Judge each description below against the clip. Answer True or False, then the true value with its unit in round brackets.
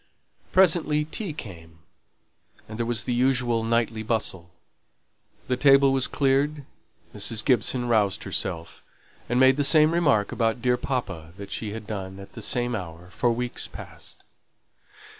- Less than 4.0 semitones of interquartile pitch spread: False (4.6 semitones)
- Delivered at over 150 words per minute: False (145 wpm)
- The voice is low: True (120 Hz)